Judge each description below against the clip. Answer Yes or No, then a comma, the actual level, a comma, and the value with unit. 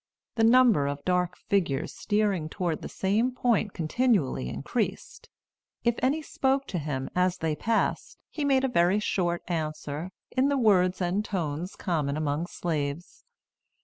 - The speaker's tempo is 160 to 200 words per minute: No, average, 145 wpm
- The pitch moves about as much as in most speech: No, wide, 6.4 semitones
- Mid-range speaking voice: Yes, medium, 180 Hz